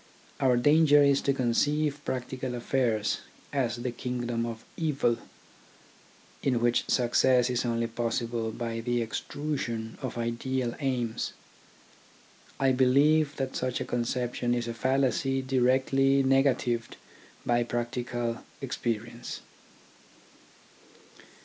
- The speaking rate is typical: No, slow, 105 wpm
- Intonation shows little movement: Yes, narrow, 2.2 semitones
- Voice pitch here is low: Yes, low, 125 Hz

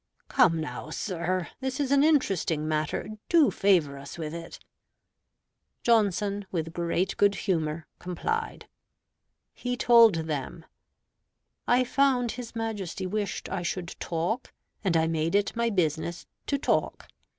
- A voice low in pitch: No, medium, 185 Hz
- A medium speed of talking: No, slow, 130 wpm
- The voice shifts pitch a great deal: Yes, wide, 6.0 semitones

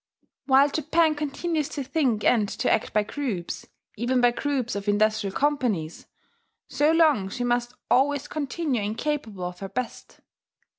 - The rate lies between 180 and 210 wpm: No, average, 145 wpm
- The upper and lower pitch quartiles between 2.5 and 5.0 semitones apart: No, wide, 5.5 semitones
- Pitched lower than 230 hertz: No, very high, 250 Hz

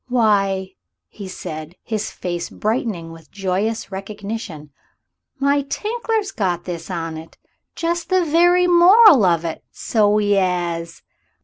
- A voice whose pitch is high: Yes, high, 205 Hz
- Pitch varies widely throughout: Yes, wide, 8.3 semitones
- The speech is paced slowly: Yes, slow, 125 wpm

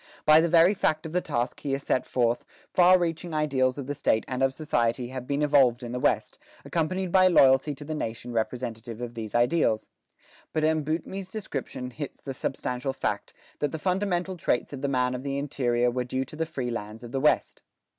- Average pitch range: Yes, average, 4.3 semitones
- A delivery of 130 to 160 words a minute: No, fast, 205 wpm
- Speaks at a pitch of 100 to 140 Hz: Yes, low, 135 Hz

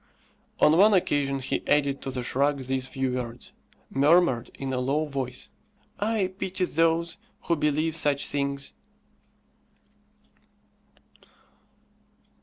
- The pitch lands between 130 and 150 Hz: Yes, medium, 140 Hz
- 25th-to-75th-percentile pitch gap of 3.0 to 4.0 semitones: Yes, average, 3.6 semitones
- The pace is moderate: No, slow, 110 wpm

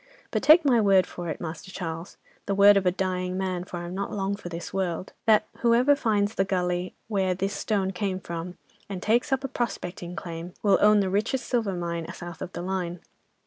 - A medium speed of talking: No, fast, 210 wpm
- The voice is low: No, high, 190 Hz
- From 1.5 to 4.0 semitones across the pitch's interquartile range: Yes, narrow, 2.6 semitones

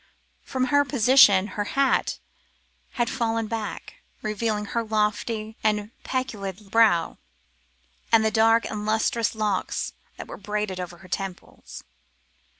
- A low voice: No, high, 215 Hz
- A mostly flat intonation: Yes, narrow, 1.8 semitones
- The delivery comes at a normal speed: No, slow, 125 wpm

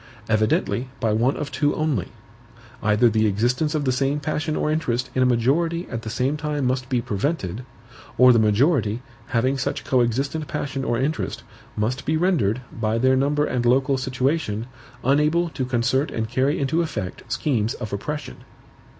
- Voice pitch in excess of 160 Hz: No, low, 130 Hz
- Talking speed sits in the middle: Yes, average, 165 wpm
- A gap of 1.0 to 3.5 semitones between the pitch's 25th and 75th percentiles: No, average, 4.2 semitones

